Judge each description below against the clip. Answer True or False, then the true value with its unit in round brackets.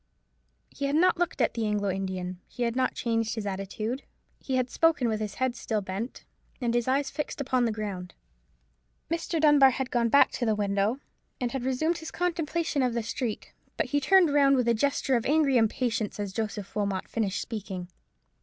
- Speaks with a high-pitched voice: True (240 Hz)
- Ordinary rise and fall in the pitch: True (4.7 semitones)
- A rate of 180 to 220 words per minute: True (195 wpm)